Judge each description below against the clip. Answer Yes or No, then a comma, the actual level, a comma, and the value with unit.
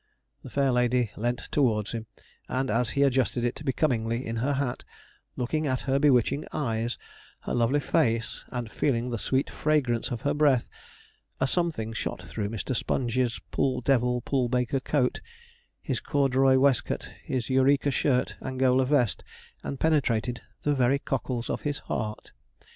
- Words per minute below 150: No, average, 155 wpm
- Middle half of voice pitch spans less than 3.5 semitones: Yes, average, 2.7 semitones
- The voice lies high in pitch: No, low, 130 Hz